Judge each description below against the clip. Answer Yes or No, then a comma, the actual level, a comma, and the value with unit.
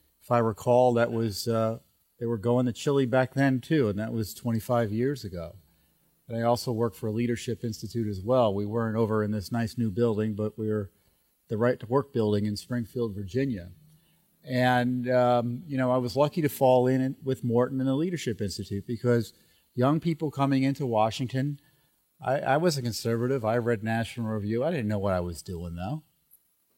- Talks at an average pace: Yes, average, 195 wpm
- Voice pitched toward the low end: Yes, low, 120 Hz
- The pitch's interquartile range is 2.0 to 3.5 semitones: Yes, average, 3.2 semitones